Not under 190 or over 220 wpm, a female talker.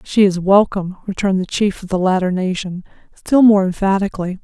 No: average, 175 wpm; female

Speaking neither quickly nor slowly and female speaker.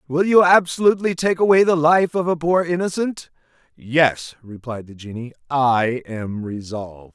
No: average, 150 wpm; male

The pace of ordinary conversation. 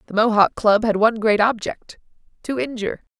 Yes: average, 150 wpm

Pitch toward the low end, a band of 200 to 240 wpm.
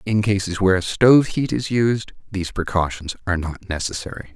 No: very low, 95 Hz; average, 165 wpm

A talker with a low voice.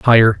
Yes: low, 115 Hz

